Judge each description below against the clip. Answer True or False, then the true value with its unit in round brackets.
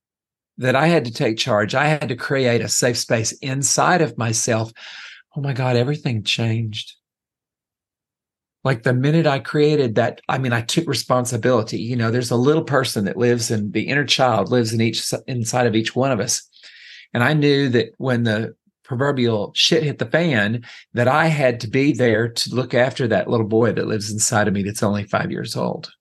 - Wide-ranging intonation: False (3.3 semitones)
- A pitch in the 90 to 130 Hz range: True (125 Hz)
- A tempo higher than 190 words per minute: True (200 wpm)